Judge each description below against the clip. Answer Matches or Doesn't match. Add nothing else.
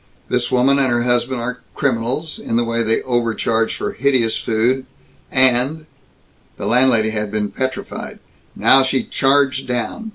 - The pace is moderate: Matches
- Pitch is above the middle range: Doesn't match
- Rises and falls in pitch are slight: Matches